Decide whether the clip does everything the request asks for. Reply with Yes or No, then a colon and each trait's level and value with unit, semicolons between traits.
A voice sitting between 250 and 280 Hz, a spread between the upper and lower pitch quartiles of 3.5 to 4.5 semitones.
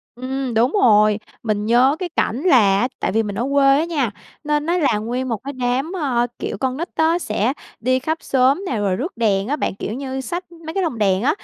No: very high, 260 Hz; average, 5.0 semitones